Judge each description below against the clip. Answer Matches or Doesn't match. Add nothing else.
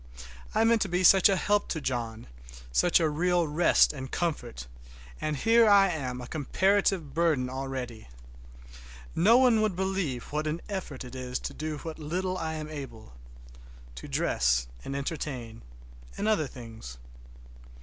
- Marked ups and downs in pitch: Matches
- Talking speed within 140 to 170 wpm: Matches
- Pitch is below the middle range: Doesn't match